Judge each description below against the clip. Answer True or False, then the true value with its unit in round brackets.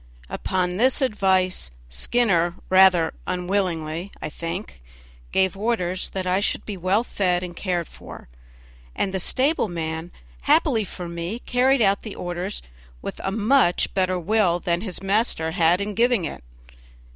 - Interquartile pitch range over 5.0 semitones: False (3.2 semitones)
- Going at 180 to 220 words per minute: False (145 wpm)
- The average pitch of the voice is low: False (185 Hz)